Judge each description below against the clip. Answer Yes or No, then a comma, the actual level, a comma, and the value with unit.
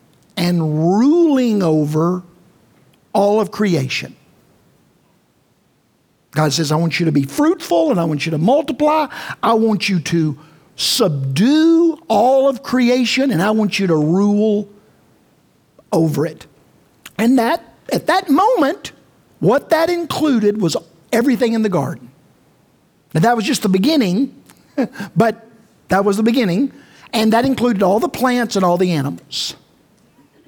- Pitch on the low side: No, high, 210 Hz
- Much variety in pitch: Yes, wide, 7.1 semitones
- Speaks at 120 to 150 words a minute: Yes, average, 140 wpm